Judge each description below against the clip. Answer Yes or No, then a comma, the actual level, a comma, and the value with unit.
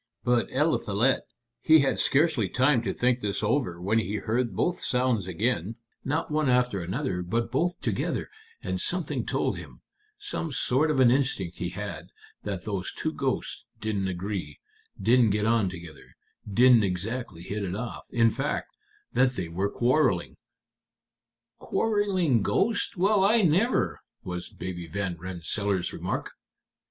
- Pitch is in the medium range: No, low, 115 Hz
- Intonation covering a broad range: Yes, wide, 6.0 semitones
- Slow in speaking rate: No, average, 145 wpm